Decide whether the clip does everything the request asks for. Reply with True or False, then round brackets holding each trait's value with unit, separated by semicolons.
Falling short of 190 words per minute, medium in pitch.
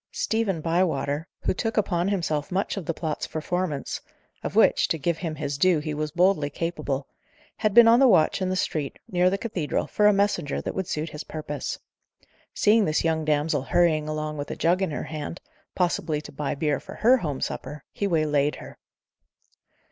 False (195 wpm; 160 Hz)